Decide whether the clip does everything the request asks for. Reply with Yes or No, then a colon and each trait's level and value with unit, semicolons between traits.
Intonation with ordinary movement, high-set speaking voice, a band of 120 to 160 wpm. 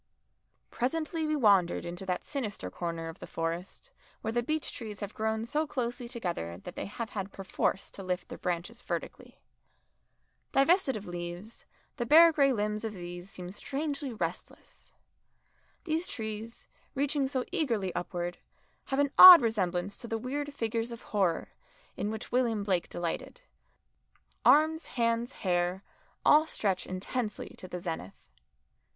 No: wide, 6.6 semitones; high, 220 Hz; average, 145 wpm